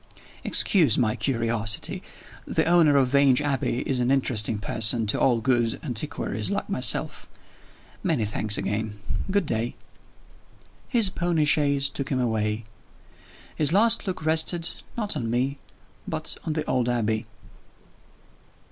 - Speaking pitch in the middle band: No, low, 130 Hz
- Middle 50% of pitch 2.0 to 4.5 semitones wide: No, wide, 5.4 semitones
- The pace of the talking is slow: Yes, slow, 130 wpm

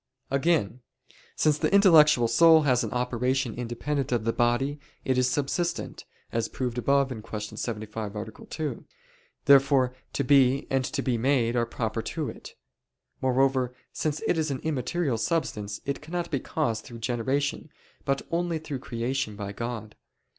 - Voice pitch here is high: No, low, 130 Hz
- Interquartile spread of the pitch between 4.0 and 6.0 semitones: No, average, 3.6 semitones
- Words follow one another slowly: No, average, 155 wpm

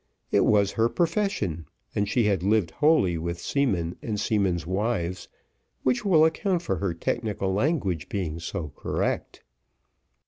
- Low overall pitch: Yes, low, 100 Hz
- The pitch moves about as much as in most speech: No, wide, 6.8 semitones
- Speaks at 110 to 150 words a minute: Yes, average, 140 wpm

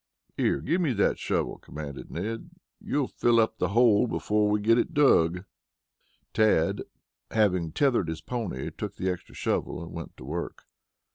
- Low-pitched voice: Yes, low, 105 Hz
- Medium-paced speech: Yes, average, 160 wpm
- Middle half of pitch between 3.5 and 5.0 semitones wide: No, wide, 5.5 semitones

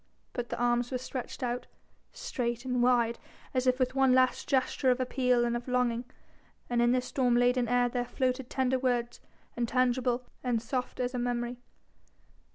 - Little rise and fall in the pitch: Yes, narrow, 1.0 semitones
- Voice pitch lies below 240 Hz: No, very high, 250 Hz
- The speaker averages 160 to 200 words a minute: Yes, average, 170 wpm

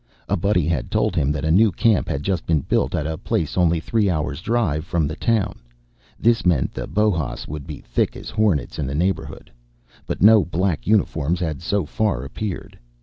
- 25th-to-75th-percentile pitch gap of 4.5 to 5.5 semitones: Yes, average, 5.1 semitones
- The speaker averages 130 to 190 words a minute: No, fast, 205 wpm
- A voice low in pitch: Yes, very low, 85 Hz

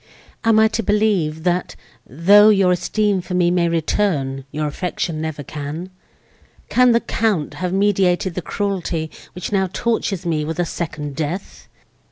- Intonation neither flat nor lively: Yes, average, 4.3 semitones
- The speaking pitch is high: No, medium, 180 Hz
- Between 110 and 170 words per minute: Yes, average, 150 wpm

